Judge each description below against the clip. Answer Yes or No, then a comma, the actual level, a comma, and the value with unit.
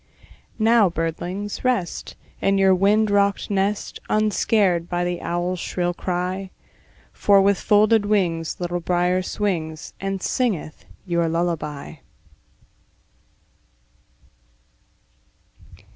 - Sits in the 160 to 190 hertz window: Yes, medium, 185 Hz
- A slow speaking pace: Yes, slow, 95 wpm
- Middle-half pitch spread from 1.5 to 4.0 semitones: Yes, average, 2.8 semitones